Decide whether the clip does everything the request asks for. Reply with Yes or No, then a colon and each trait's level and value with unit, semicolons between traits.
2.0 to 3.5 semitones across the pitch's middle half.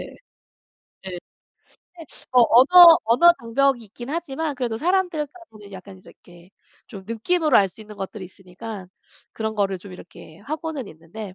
No: wide, 7.5 semitones